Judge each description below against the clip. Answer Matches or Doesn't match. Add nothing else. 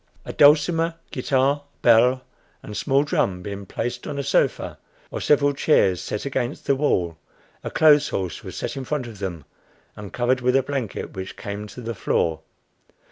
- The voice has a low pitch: Matches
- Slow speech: Doesn't match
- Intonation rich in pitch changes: Matches